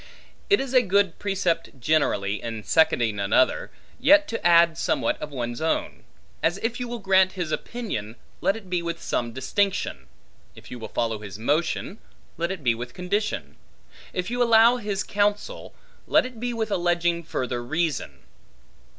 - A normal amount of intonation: No, wide, 8.3 semitones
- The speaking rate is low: No, average, 165 wpm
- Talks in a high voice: No, medium, 175 Hz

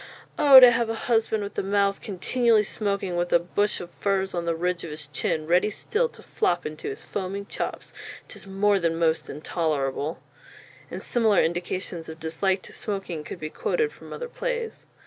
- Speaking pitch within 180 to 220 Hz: Yes, high, 190 Hz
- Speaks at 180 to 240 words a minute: Yes, average, 185 wpm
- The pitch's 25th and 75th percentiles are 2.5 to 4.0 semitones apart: No, average, 4.4 semitones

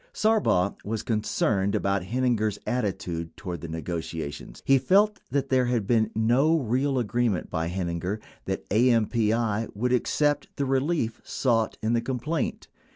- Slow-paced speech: No, average, 145 wpm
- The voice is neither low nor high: No, low, 115 Hz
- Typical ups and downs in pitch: Yes, average, 4.6 semitones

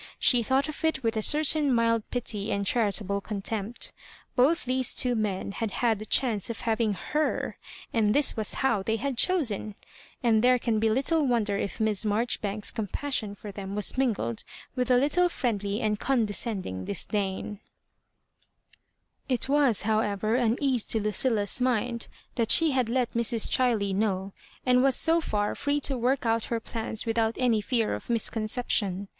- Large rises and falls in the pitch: No, average, 3.4 semitones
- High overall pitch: Yes, high, 225 Hz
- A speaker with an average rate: Yes, average, 170 wpm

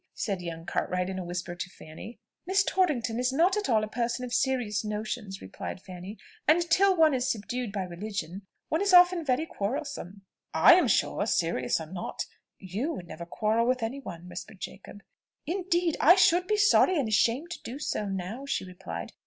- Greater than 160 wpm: Yes, average, 190 wpm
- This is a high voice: Yes, high, 225 Hz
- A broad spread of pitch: Yes, wide, 8.9 semitones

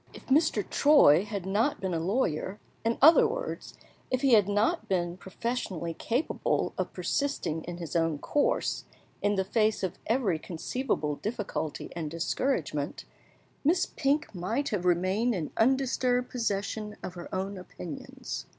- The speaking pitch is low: No, high, 205 Hz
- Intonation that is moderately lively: No, wide, 6.5 semitones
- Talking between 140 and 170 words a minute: Yes, average, 145 wpm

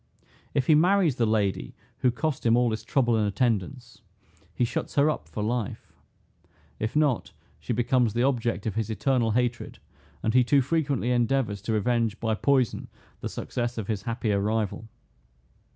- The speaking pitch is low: Yes, low, 120 Hz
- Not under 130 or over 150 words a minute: No, average, 170 wpm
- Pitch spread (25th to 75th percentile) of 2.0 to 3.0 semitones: Yes, average, 2.7 semitones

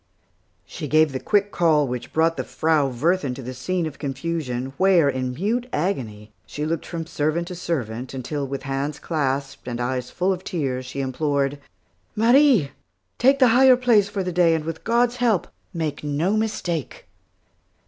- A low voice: No, medium, 155 Hz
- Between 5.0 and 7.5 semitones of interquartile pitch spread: Yes, wide, 5.5 semitones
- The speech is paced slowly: No, average, 170 wpm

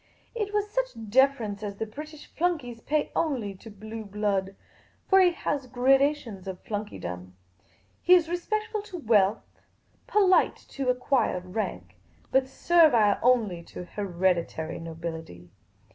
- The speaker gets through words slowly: Yes, slow, 130 wpm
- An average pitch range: No, wide, 8.0 semitones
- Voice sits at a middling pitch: No, high, 225 Hz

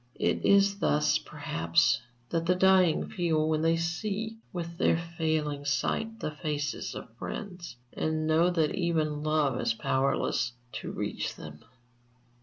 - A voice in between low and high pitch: Yes, medium, 160 Hz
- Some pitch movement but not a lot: Yes, average, 3.1 semitones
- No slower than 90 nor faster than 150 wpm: Yes, average, 140 wpm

